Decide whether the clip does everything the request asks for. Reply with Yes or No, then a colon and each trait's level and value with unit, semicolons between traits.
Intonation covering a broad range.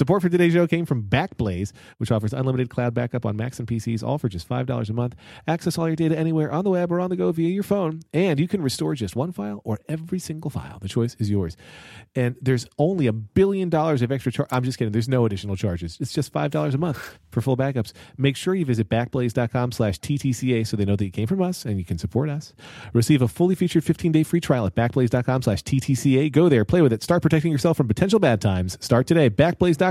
Yes: wide, 5.9 semitones